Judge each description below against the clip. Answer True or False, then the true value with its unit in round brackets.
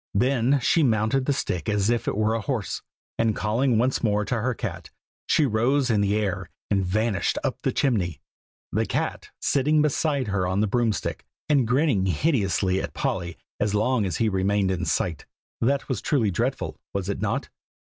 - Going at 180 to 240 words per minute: True (190 wpm)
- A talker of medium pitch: False (110 Hz)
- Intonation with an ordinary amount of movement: True (4.7 semitones)